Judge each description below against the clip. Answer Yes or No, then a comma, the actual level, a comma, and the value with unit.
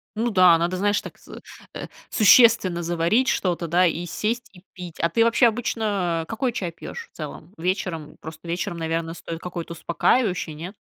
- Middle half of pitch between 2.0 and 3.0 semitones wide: No, average, 4.3 semitones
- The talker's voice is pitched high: No, medium, 180 Hz